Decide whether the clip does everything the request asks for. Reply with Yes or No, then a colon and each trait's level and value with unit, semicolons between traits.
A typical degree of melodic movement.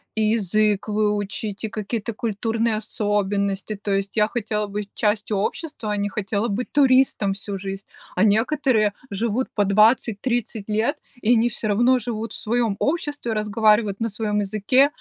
No: narrow, 2.2 semitones